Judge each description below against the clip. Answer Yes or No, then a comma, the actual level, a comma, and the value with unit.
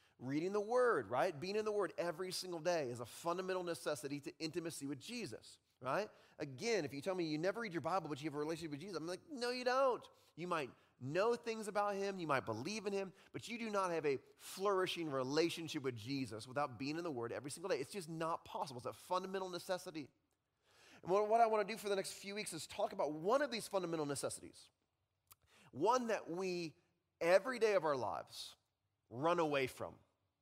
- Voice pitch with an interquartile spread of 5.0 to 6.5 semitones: Yes, wide, 5.5 semitones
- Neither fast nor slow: No, fast, 215 wpm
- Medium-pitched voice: Yes, medium, 175 Hz